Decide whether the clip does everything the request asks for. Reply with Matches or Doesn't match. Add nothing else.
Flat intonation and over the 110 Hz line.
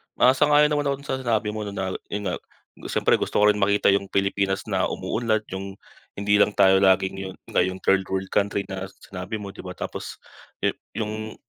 Doesn't match